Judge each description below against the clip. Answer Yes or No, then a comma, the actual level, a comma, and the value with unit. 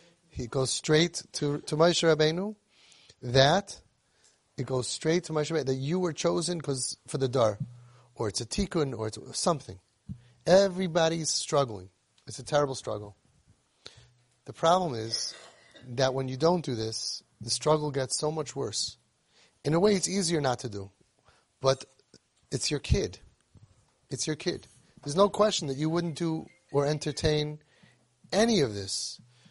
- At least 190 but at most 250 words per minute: No, average, 155 wpm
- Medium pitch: Yes, medium, 145 Hz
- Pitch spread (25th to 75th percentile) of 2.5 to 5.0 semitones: No, wide, 5.4 semitones